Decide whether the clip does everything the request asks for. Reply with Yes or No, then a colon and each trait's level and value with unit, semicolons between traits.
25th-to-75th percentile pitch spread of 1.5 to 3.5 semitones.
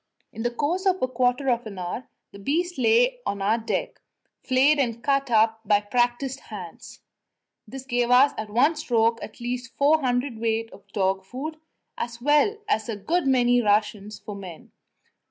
No: average, 4.2 semitones